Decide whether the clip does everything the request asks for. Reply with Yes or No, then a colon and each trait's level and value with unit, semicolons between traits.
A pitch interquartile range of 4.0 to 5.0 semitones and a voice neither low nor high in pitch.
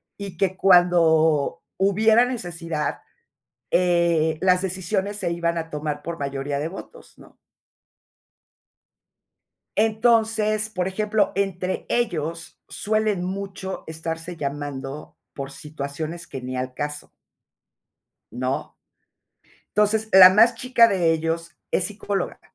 Yes: average, 4.5 semitones; medium, 175 Hz